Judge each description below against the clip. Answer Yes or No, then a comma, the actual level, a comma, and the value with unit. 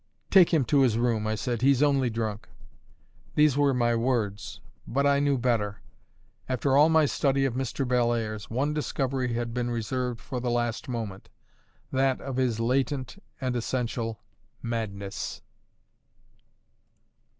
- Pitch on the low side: Yes, low, 125 Hz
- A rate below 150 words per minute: Yes, average, 140 wpm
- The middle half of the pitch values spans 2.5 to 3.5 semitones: Yes, average, 2.8 semitones